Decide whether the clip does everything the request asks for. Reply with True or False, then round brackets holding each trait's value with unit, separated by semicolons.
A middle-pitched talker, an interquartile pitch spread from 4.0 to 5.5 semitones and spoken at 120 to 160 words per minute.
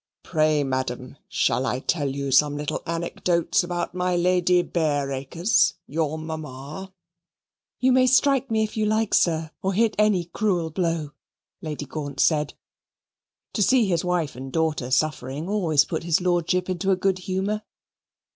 True (170 Hz; 4.3 semitones; 150 wpm)